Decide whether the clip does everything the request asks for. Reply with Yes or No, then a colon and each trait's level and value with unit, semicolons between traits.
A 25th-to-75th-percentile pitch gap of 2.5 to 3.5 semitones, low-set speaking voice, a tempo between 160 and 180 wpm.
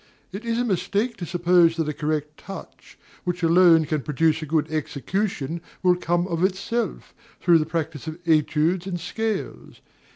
No: average, 2.9 semitones; medium, 170 Hz; average, 165 wpm